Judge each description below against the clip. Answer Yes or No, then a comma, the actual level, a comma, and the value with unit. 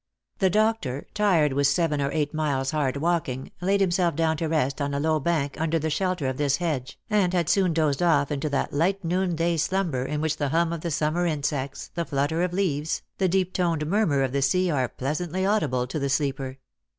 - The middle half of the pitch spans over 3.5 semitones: Yes, average, 3.9 semitones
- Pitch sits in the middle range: Yes, medium, 155 Hz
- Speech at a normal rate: No, fast, 220 wpm